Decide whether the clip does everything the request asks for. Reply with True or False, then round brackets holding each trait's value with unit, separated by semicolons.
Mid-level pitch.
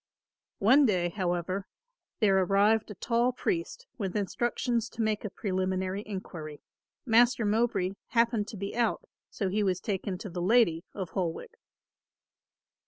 False (205 Hz)